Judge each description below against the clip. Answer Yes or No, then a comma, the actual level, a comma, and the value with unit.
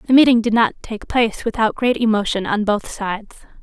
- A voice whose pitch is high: Yes, high, 220 Hz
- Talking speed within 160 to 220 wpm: Yes, average, 200 wpm